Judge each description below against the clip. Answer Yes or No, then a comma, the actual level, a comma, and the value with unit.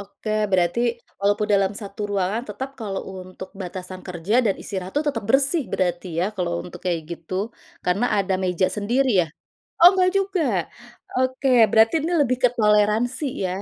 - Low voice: No, high, 205 Hz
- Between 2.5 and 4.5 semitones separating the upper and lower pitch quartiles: No, average, 5.1 semitones